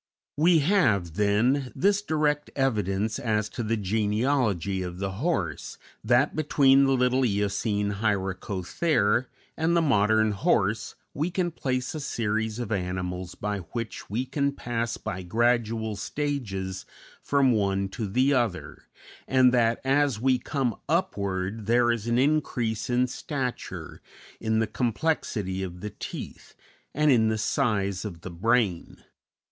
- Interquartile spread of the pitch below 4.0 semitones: No, average, 4.9 semitones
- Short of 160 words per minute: Yes, average, 140 wpm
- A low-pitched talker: Yes, low, 115 Hz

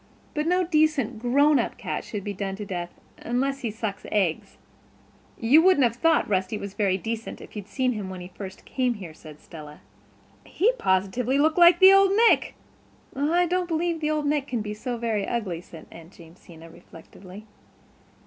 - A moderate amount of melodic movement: No, wide, 8.1 semitones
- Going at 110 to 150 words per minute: No, average, 170 wpm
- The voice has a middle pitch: No, high, 230 Hz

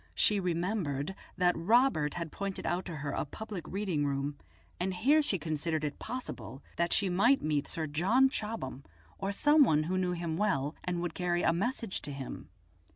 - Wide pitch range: No, average, 5.0 semitones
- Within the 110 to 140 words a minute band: No, average, 185 wpm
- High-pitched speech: No, medium, 175 Hz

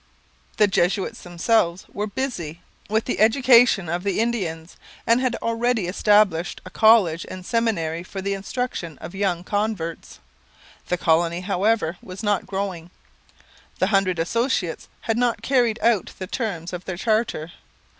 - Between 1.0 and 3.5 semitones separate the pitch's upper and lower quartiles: No, average, 4.6 semitones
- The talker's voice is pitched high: Yes, high, 195 Hz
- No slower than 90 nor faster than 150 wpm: Yes, average, 145 wpm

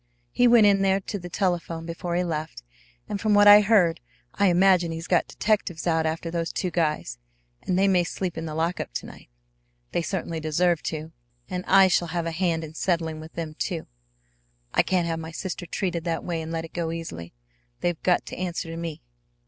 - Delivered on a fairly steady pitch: Yes, narrow, 2.2 semitones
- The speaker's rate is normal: No, fast, 210 wpm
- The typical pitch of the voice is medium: Yes, medium, 170 Hz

